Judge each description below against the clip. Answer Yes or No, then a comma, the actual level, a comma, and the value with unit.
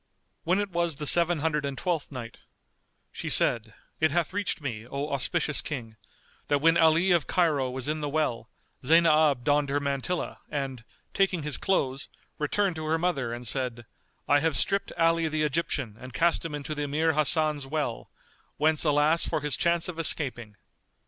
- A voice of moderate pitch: Yes, medium, 150 Hz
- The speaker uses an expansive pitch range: No, average, 3.3 semitones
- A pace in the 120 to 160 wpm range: No, average, 175 wpm